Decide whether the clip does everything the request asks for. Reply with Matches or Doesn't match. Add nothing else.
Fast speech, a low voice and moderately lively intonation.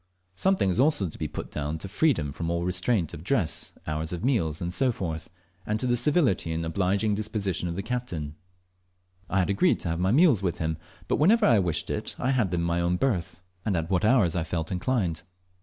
Doesn't match